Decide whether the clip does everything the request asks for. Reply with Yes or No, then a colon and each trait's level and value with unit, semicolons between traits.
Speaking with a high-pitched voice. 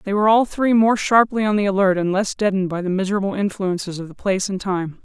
Yes: high, 195 Hz